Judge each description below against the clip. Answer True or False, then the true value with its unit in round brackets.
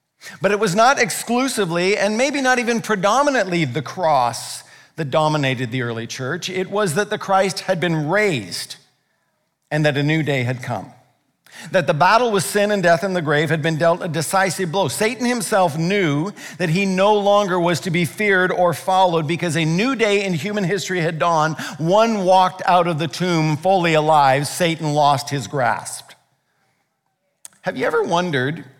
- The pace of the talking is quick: False (180 wpm)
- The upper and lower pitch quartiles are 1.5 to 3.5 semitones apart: False (4.4 semitones)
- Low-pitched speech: False (180 Hz)